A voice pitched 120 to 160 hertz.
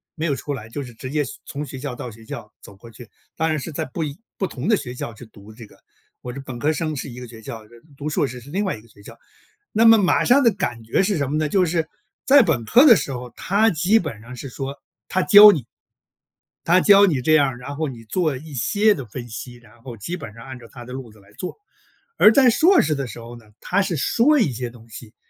Yes: medium, 140 Hz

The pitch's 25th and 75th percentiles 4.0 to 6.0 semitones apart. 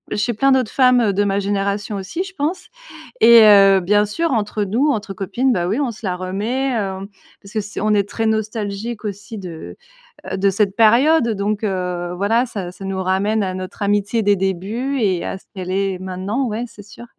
No: average, 3.0 semitones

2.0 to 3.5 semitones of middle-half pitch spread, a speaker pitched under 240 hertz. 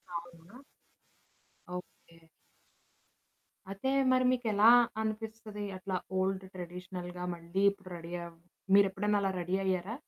Yes: average, 2.8 semitones; high, 190 Hz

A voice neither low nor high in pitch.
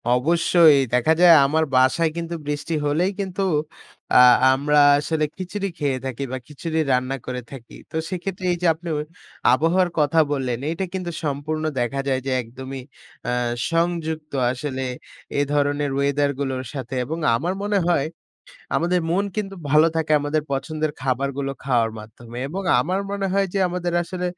Yes: medium, 150 Hz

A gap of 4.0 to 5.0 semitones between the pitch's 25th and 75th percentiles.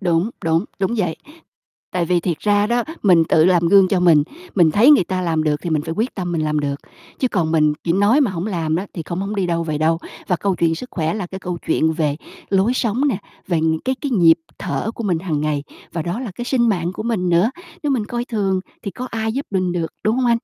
Yes: average, 4.6 semitones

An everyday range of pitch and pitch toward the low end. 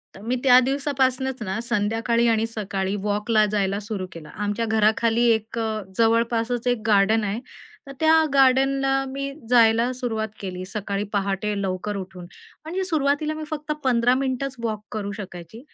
No: average, 3.7 semitones; high, 225 Hz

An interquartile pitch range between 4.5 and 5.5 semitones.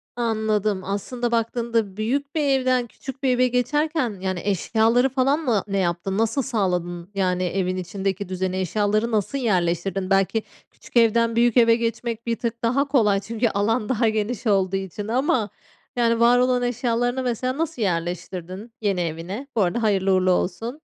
No: average, 4.1 semitones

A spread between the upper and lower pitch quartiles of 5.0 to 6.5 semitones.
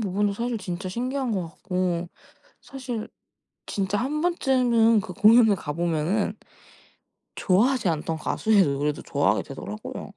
Yes: wide, 5.4 semitones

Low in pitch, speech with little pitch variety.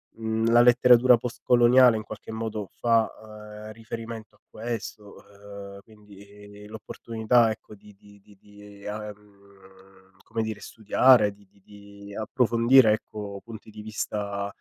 Yes: low, 105 Hz; narrow, 1.9 semitones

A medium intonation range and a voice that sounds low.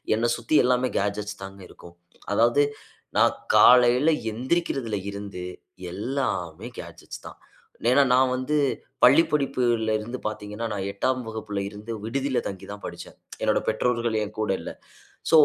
Yes: average, 3.8 semitones; low, 115 Hz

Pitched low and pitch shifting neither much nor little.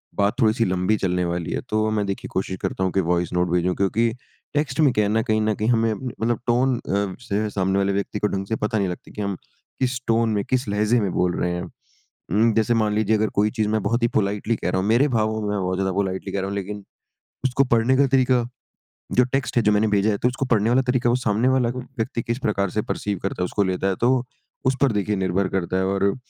Yes: low, 105 Hz; average, 3.2 semitones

